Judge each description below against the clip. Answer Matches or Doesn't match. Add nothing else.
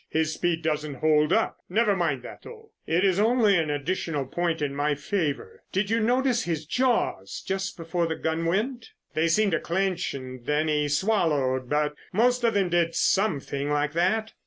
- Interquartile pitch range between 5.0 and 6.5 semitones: Matches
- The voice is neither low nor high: Matches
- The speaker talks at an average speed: Matches